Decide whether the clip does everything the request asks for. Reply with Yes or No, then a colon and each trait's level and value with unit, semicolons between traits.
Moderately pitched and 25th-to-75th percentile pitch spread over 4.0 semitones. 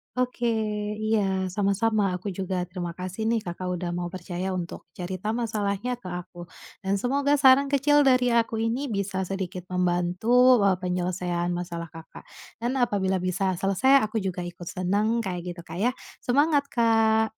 No: high, 195 Hz; average, 4.5 semitones